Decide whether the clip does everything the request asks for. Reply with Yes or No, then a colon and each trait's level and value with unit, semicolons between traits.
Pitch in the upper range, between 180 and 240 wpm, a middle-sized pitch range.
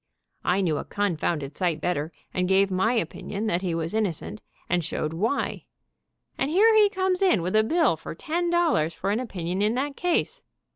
No: high, 200 Hz; average, 195 wpm; wide, 8.8 semitones